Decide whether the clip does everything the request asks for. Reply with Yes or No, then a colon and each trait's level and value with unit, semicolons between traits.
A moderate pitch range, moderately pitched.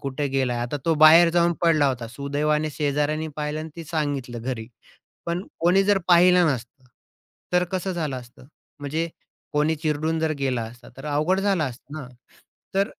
Yes: average, 3.7 semitones; medium, 150 Hz